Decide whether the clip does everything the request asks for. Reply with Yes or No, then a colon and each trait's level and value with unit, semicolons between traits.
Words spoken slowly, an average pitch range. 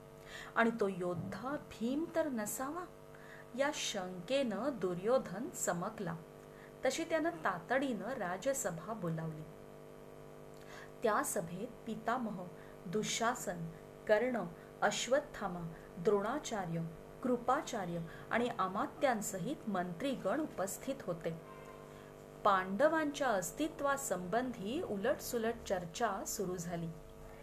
No: slow, 75 wpm; wide, 5.8 semitones